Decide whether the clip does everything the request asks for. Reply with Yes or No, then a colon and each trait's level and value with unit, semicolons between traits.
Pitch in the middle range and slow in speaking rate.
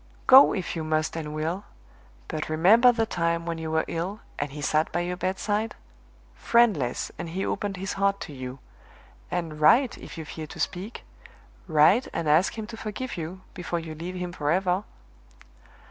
No: medium, 175 Hz; average, 175 wpm